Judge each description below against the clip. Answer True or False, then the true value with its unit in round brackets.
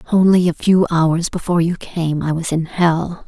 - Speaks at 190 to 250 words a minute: True (200 wpm)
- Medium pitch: True (170 Hz)